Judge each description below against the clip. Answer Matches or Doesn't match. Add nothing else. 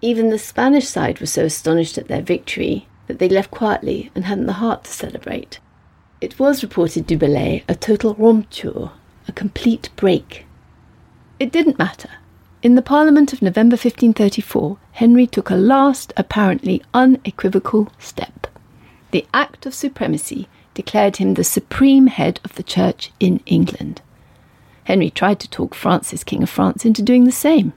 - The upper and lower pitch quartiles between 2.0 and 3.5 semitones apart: Doesn't match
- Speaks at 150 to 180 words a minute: Matches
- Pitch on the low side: Doesn't match